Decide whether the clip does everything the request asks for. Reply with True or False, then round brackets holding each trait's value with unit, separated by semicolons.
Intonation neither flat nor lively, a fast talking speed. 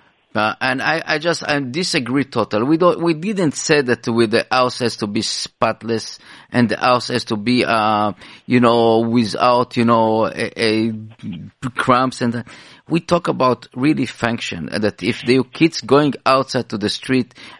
False (3.6 semitones; 175 wpm)